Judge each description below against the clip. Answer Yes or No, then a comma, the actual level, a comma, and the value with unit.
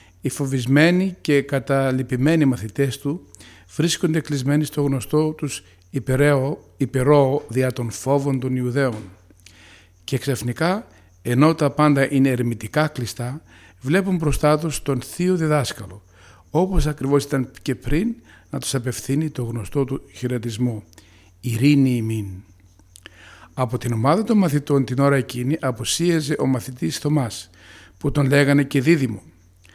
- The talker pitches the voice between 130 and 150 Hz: Yes, low, 135 Hz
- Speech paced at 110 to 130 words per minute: Yes, average, 125 wpm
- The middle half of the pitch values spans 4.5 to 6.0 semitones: Yes, average, 4.8 semitones